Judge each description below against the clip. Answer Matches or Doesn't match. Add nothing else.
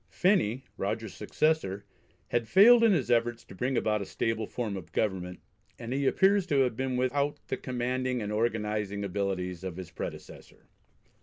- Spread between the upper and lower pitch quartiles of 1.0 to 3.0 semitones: Doesn't match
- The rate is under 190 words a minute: Matches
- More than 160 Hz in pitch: Doesn't match